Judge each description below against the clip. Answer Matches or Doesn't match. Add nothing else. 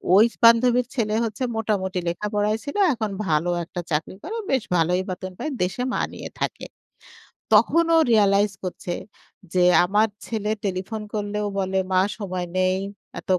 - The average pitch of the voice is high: Matches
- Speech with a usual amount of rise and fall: Matches